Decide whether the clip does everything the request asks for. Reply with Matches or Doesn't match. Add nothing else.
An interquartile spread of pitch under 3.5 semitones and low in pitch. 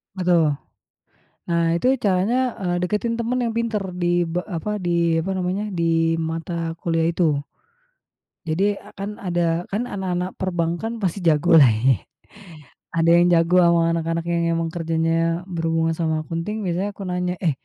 Doesn't match